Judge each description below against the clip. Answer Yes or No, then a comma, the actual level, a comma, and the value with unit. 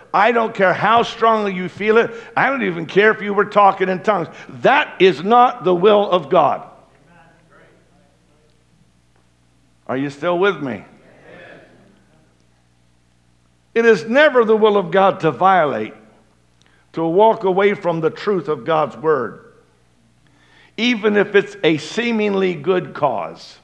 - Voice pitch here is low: No, medium, 185 Hz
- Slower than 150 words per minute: Yes, average, 140 wpm